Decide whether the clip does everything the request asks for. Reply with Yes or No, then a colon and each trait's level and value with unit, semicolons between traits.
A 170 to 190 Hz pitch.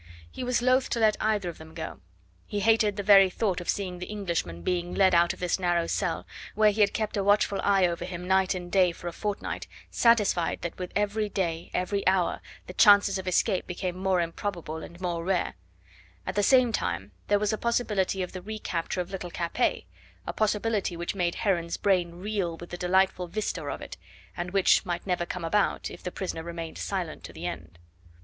Yes: medium, 185 Hz